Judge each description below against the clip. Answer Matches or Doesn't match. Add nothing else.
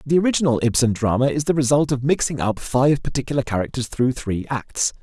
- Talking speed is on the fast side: Doesn't match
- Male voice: Matches